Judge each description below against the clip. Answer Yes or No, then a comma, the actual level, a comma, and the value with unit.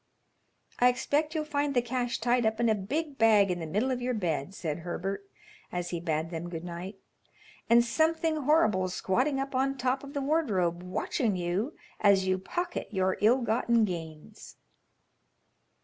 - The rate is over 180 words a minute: No, average, 170 wpm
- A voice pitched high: Yes, high, 220 Hz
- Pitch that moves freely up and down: Yes, wide, 6.5 semitones